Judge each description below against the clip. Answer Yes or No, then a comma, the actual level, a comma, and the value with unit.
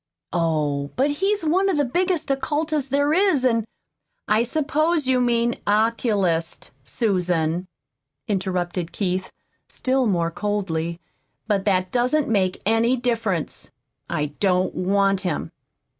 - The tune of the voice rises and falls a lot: Yes, wide, 7.0 semitones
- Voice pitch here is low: No, high, 215 Hz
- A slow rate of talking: Yes, slow, 125 wpm